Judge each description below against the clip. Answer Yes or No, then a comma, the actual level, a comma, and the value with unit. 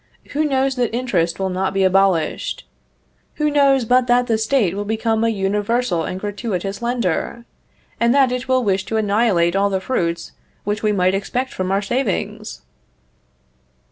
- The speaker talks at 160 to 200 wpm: Yes, average, 165 wpm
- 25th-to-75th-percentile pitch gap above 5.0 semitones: No, average, 4.3 semitones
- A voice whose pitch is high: Yes, high, 210 Hz